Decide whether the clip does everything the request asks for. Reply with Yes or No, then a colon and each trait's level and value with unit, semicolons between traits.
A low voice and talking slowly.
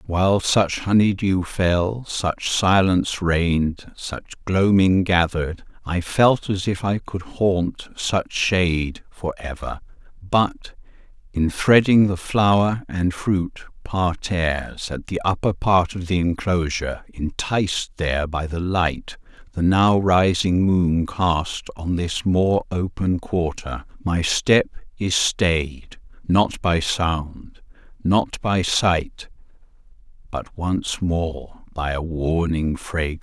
Yes: very low, 90 Hz; slow, 125 wpm